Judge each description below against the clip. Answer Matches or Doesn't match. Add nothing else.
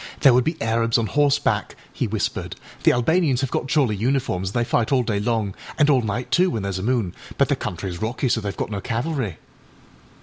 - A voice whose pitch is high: Doesn't match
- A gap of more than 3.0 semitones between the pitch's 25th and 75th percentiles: Matches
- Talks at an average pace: Doesn't match